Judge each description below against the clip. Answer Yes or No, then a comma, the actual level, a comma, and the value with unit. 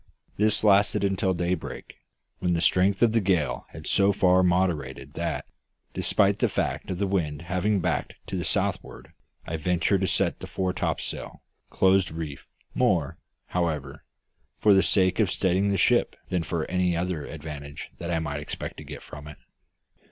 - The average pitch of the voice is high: No, very low, 90 Hz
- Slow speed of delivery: No, average, 165 wpm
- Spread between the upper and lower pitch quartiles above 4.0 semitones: No, average, 3.1 semitones